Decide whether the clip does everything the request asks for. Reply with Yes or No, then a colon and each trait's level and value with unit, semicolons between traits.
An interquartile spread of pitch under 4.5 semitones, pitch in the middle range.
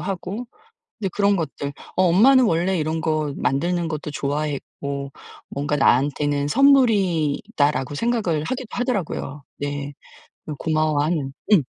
No: average, 5.3 semitones; medium, 155 Hz